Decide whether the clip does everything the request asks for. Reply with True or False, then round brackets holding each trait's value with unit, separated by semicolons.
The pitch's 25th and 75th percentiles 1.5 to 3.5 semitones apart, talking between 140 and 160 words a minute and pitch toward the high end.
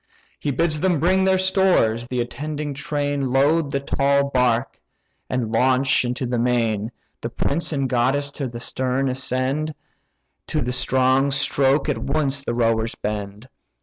False (2.7 semitones; 150 wpm; 135 Hz)